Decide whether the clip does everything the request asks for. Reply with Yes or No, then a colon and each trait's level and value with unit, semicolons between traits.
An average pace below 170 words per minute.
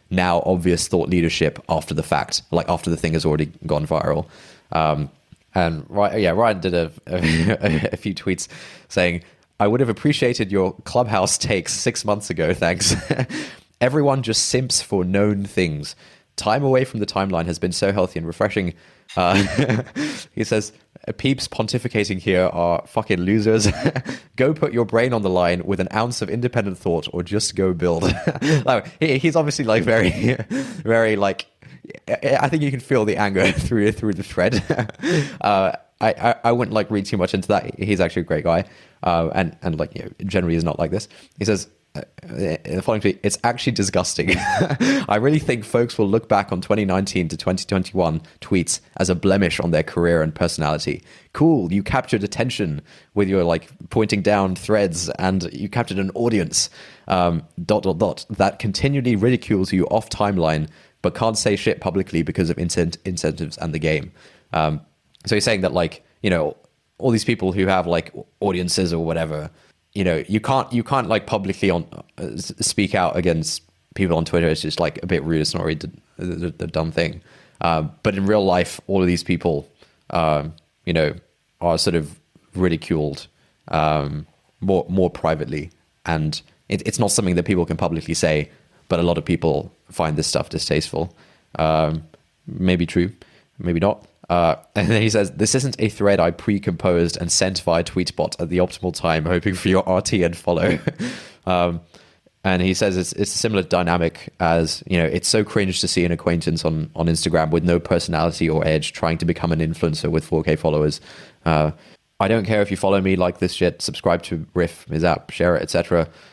No: average, 185 wpm